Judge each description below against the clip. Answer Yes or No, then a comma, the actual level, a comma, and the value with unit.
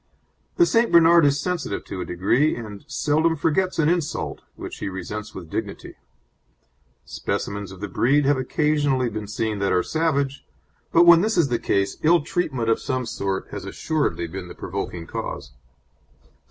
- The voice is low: Yes, low, 130 Hz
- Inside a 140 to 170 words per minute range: Yes, average, 165 wpm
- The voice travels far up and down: Yes, wide, 8.1 semitones